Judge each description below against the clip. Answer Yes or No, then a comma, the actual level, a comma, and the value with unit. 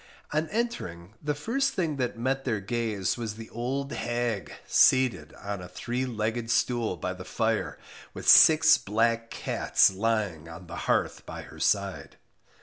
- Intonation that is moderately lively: Yes, average, 4.7 semitones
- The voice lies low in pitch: Yes, low, 115 Hz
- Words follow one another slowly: No, average, 155 wpm